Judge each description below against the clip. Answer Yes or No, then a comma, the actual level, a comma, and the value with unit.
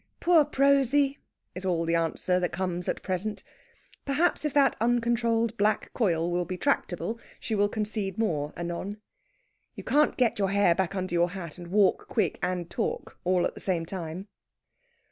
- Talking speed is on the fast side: No, average, 170 wpm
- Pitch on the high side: Yes, high, 195 Hz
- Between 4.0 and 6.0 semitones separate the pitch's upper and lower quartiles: Yes, average, 4.8 semitones